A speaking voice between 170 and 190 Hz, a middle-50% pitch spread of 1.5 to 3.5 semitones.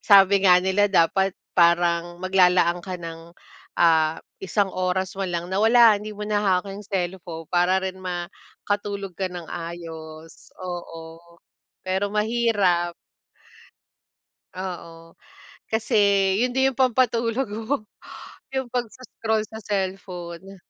Yes: medium, 185 Hz; average, 3.2 semitones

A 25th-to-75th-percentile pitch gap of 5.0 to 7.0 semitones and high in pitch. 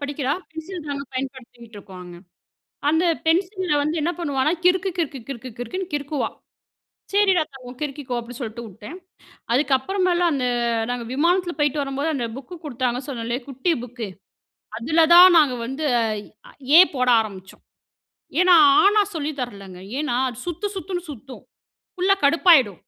Yes: wide, 5.6 semitones; very high, 280 Hz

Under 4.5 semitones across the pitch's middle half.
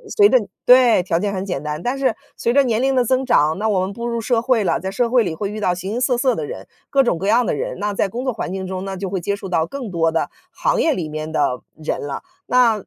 No: wide, 5.4 semitones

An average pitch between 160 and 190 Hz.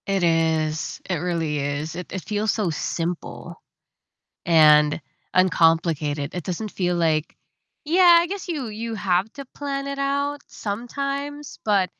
Yes: medium, 185 Hz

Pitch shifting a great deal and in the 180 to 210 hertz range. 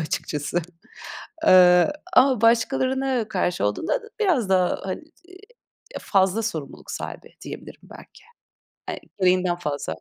Yes: wide, 6.6 semitones; high, 190 Hz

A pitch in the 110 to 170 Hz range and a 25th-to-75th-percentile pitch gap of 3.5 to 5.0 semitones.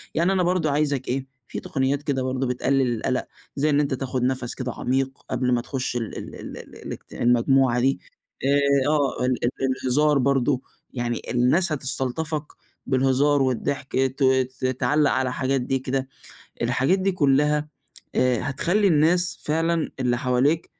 No: low, 135 Hz; narrow, 2.5 semitones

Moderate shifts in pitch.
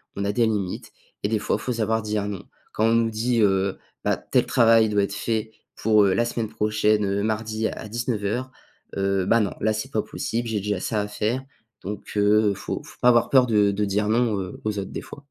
No: narrow, 1.9 semitones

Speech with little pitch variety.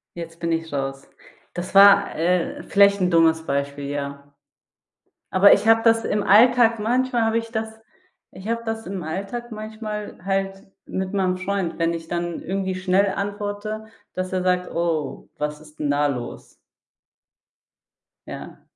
No: average, 4.4 semitones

